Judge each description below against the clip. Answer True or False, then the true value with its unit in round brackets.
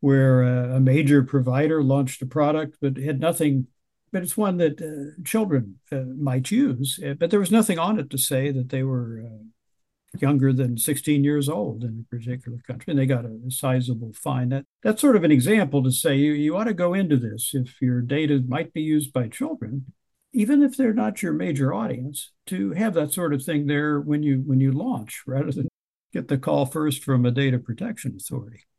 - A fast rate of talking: True (210 wpm)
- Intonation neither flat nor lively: True (3.2 semitones)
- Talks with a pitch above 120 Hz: True (140 Hz)